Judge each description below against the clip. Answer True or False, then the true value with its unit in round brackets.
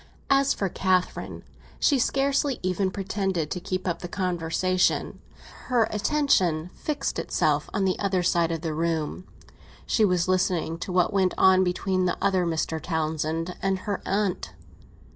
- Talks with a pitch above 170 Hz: True (185 Hz)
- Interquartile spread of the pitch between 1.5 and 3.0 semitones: True (2.7 semitones)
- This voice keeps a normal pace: True (155 wpm)